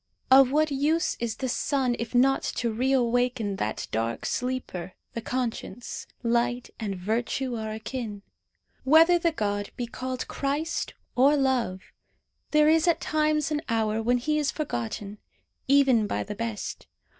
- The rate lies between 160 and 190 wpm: No, average, 145 wpm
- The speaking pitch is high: Yes, high, 245 Hz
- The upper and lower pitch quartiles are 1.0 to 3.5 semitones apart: No, average, 4.1 semitones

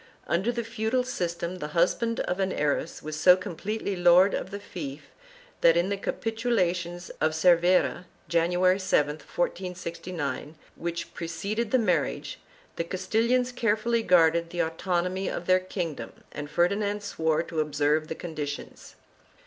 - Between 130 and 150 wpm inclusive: Yes, average, 140 wpm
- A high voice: No, medium, 175 Hz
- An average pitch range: Yes, average, 3.5 semitones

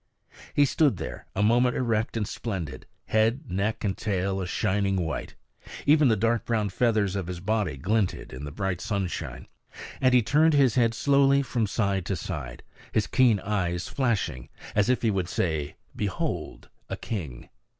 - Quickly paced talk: No, average, 170 wpm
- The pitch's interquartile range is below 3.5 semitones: No, average, 4.2 semitones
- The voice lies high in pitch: No, low, 105 Hz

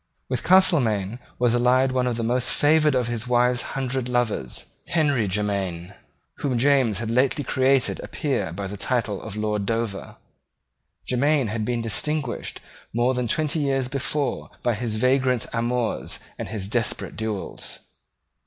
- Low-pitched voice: Yes, low, 120 Hz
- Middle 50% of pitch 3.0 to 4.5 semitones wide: Yes, average, 3.4 semitones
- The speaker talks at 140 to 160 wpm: Yes, average, 150 wpm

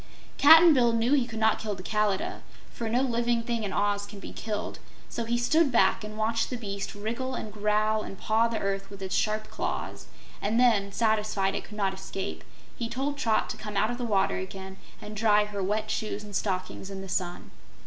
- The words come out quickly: Yes, fast, 215 wpm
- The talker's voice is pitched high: Yes, high, 215 Hz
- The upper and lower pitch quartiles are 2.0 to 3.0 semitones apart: Yes, average, 2.7 semitones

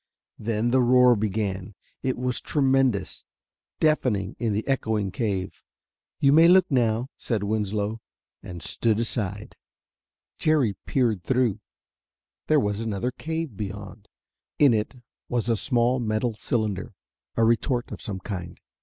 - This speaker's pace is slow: Yes, slow, 130 wpm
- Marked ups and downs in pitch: No, average, 3.7 semitones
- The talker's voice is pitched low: Yes, low, 115 Hz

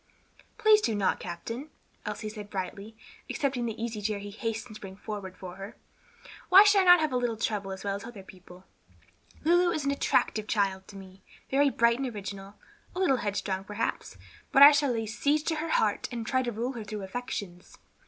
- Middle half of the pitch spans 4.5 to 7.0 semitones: Yes, wide, 5.4 semitones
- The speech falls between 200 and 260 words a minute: Yes, fast, 205 wpm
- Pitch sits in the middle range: No, high, 220 Hz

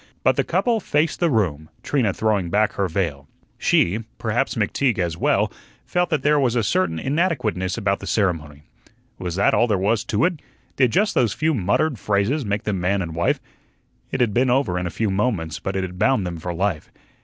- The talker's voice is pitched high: No, low, 100 Hz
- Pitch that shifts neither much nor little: No, wide, 6.3 semitones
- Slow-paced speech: No, fast, 205 wpm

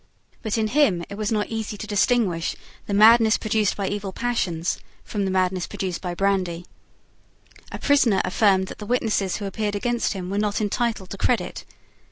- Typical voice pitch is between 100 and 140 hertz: No, high, 205 Hz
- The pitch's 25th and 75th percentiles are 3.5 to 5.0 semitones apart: No, average, 2.8 semitones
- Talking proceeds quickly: No, average, 180 wpm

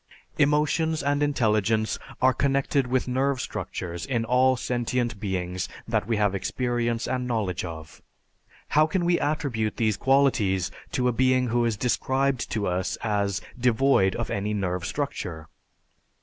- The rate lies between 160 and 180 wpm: No, average, 145 wpm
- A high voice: No, low, 120 Hz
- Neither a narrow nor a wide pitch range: Yes, average, 4.6 semitones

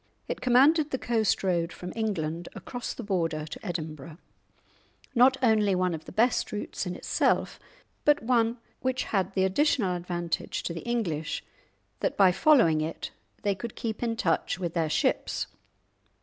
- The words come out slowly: No, average, 160 wpm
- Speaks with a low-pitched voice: No, high, 195 Hz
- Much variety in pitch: Yes, wide, 5.9 semitones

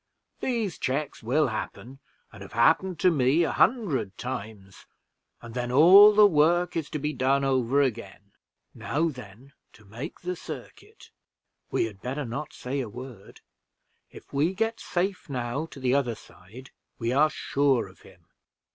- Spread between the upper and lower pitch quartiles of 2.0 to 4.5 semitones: No, average, 5.1 semitones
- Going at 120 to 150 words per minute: No, average, 160 wpm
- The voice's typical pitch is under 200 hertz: Yes, low, 135 Hz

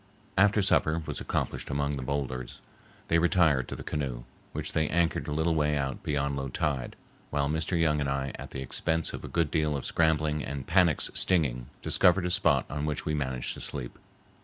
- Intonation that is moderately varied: Yes, average, 3.0 semitones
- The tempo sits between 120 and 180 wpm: No, average, 200 wpm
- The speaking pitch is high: No, very low, 75 Hz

